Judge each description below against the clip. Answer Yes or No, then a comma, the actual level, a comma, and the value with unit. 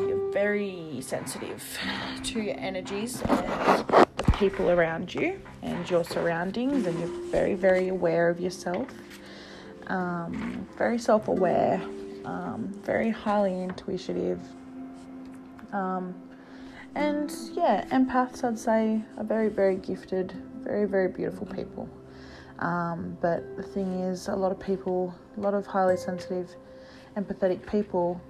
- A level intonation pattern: No, average, 3.9 semitones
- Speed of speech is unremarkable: No, slow, 125 wpm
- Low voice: No, medium, 185 Hz